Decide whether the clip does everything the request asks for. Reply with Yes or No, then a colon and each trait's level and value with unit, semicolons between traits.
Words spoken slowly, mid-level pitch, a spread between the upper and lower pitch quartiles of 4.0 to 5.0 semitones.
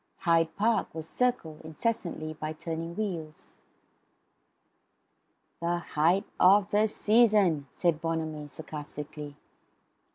Yes: slow, 95 wpm; medium, 165 Hz; average, 4.3 semitones